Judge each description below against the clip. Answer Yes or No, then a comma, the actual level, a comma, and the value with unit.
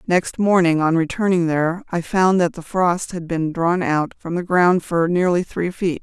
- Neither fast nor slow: No, fast, 210 wpm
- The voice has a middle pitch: Yes, medium, 175 Hz